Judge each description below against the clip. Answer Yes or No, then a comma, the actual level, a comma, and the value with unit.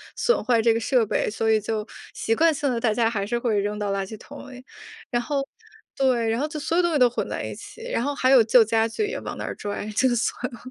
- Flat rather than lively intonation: No, average, 3.7 semitones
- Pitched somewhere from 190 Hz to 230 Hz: No, high, 240 Hz